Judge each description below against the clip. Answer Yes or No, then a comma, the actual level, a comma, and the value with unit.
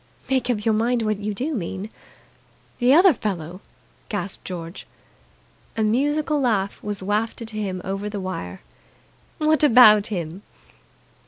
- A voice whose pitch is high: Yes, high, 215 Hz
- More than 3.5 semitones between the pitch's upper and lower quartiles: Yes, average, 4.2 semitones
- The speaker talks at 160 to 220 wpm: No, average, 140 wpm